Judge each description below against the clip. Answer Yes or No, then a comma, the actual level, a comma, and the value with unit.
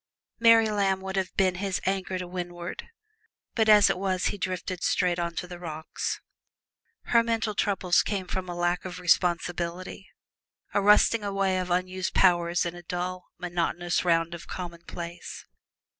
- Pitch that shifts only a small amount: Yes, narrow, 1.8 semitones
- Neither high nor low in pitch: Yes, medium, 180 Hz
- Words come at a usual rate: Yes, average, 160 wpm